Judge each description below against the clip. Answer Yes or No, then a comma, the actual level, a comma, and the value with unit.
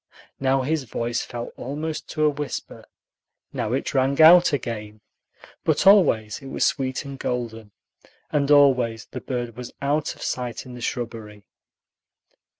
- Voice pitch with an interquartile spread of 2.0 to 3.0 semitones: No, average, 3.5 semitones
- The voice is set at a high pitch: No, low, 130 Hz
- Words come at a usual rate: Yes, average, 150 wpm